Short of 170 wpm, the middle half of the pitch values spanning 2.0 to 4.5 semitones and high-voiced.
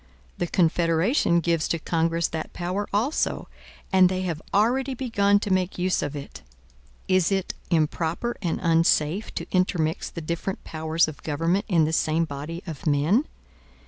No: average, 155 wpm; average, 3.1 semitones; medium, 170 Hz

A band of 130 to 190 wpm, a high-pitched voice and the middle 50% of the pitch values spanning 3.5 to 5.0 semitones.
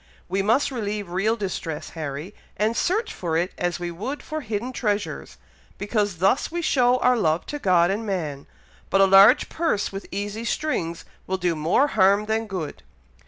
Yes: average, 175 wpm; high, 200 Hz; average, 4.7 semitones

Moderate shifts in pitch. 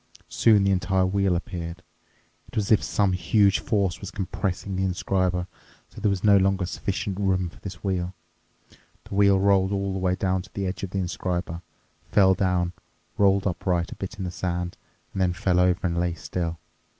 No: narrow, 1.6 semitones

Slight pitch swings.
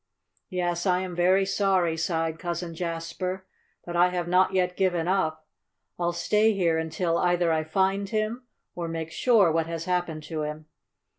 Yes: narrow, 2.3 semitones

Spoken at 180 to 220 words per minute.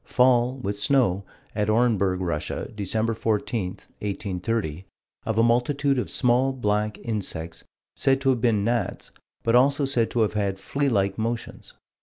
No: average, 150 wpm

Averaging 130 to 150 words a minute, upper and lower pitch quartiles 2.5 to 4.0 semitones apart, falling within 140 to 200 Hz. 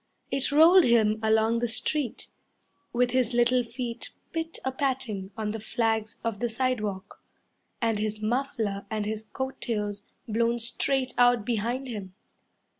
No: average, 145 wpm; average, 2.9 semitones; high, 230 Hz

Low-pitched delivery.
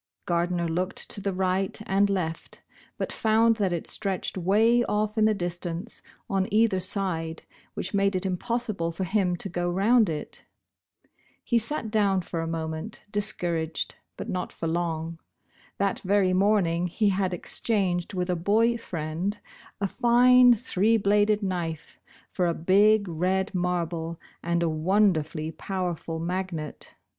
No: medium, 185 Hz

